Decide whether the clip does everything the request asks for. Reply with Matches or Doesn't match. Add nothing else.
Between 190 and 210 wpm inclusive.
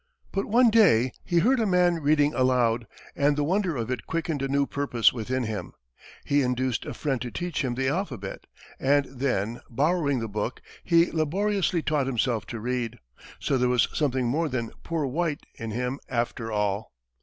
Doesn't match